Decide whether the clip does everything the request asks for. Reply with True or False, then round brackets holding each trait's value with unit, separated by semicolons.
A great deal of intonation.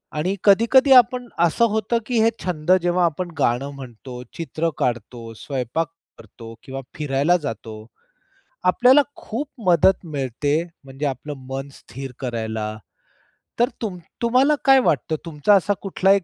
True (7.7 semitones)